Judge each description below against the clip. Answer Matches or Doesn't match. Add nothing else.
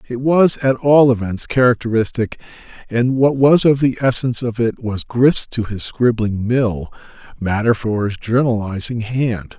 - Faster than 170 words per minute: Doesn't match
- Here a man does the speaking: Matches